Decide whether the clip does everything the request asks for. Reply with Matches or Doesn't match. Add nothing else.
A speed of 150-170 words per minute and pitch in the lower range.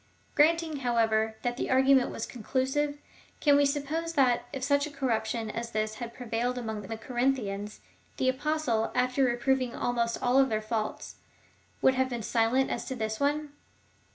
Doesn't match